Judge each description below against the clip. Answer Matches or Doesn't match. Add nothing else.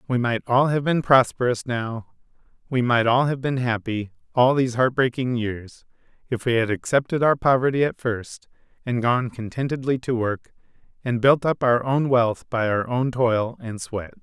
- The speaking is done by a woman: Doesn't match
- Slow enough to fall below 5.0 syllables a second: Matches